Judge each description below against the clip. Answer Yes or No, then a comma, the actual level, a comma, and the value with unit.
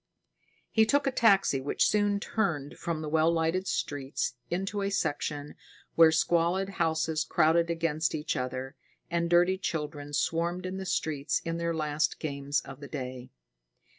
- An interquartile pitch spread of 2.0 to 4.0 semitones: Yes, average, 3.7 semitones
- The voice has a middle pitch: Yes, medium, 165 Hz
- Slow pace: No, average, 155 wpm